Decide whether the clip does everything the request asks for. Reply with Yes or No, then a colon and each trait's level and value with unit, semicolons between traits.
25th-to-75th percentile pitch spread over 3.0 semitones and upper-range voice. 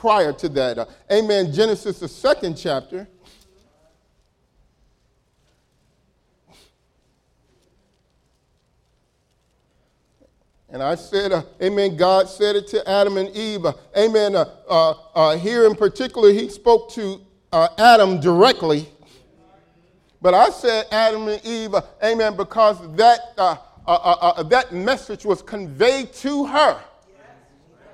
Yes: average, 3.5 semitones; high, 205 Hz